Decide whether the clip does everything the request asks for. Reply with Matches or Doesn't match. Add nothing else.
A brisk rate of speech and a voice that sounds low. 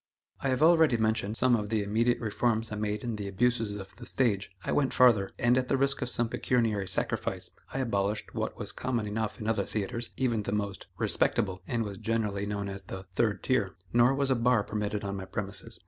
Matches